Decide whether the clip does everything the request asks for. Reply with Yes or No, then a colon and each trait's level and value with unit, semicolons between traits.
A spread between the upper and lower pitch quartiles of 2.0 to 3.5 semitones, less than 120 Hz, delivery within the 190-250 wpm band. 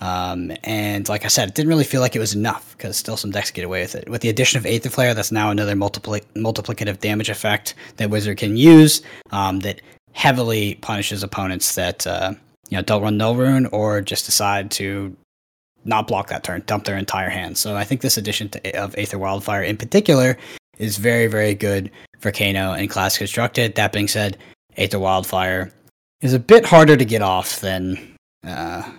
Yes: narrow, 2.5 semitones; low, 105 Hz; average, 200 wpm